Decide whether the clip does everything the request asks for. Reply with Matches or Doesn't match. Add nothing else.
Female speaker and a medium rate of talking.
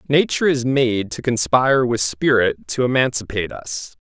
Doesn't match